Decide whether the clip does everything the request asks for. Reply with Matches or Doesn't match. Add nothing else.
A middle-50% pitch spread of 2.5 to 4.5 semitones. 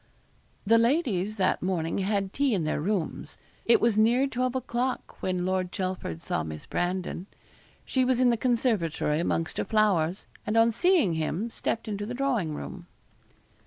Doesn't match